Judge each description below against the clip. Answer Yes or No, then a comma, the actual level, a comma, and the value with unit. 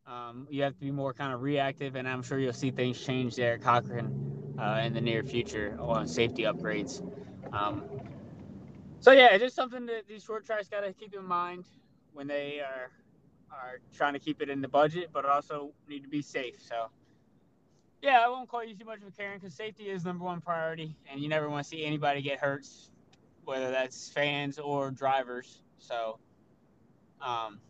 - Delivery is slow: No, average, 200 wpm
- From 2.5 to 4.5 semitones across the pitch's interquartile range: No, wide, 5.6 semitones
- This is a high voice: No, medium, 140 Hz